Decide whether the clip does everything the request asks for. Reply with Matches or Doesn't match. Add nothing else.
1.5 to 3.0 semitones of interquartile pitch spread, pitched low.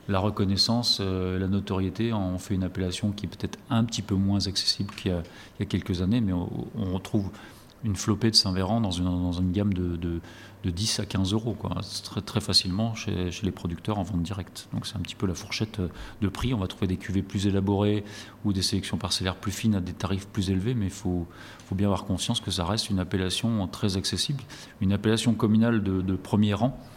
Matches